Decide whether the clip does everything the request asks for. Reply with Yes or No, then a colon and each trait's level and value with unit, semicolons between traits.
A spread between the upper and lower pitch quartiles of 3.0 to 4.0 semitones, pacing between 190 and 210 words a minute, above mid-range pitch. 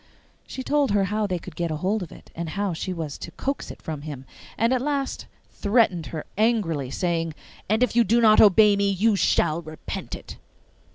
No: average, 5.3 semitones; fast, 205 wpm; high, 200 Hz